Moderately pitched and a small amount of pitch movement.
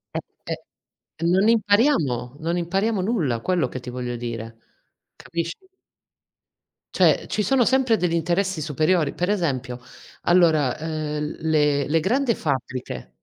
No: medium, 160 Hz; wide, 6.1 semitones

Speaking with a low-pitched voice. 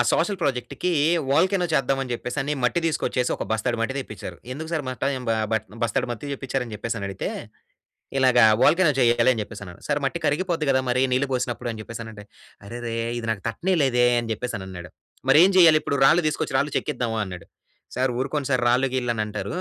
Yes: low, 125 Hz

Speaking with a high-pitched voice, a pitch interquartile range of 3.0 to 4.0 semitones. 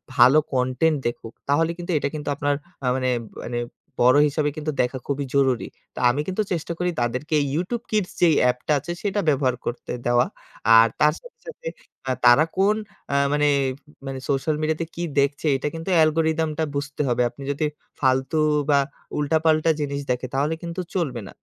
No: medium, 150 Hz; average, 3.6 semitones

